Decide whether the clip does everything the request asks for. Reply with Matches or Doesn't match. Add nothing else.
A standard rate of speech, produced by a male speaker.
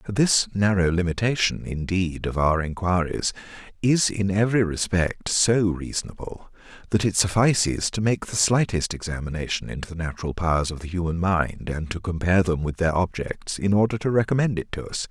Matches